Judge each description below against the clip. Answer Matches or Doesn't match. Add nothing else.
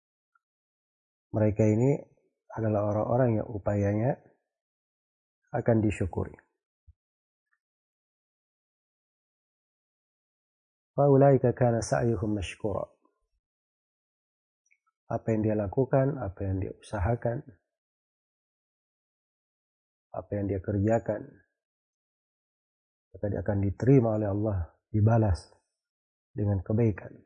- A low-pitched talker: Matches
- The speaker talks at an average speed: Doesn't match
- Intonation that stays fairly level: Doesn't match